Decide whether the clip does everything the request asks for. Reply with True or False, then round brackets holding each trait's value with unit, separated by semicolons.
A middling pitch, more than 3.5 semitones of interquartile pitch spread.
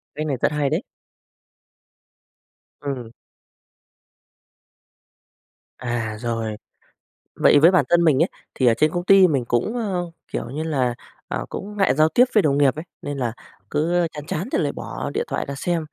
True (150 Hz; 5.0 semitones)